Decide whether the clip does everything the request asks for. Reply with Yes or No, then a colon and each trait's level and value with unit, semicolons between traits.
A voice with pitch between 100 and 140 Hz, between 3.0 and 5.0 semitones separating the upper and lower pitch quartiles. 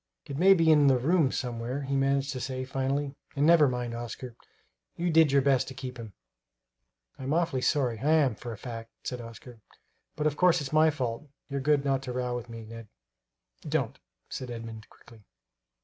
Yes: low, 135 Hz; average, 3.4 semitones